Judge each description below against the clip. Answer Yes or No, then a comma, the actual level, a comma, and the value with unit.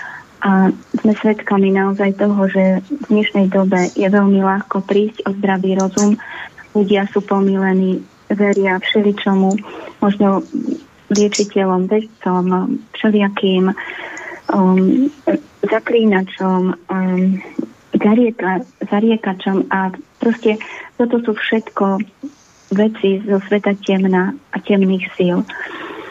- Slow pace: Yes, slow, 95 wpm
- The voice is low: No, high, 200 Hz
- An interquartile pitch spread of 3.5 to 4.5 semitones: No, narrow, 2.4 semitones